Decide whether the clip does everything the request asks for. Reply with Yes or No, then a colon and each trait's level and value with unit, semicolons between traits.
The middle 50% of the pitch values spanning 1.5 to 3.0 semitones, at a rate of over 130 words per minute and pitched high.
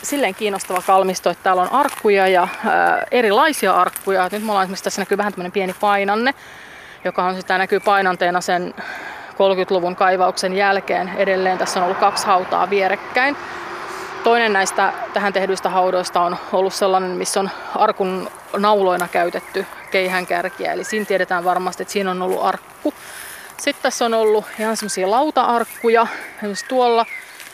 Yes: narrow, 2.6 semitones; average, 150 wpm; high, 195 Hz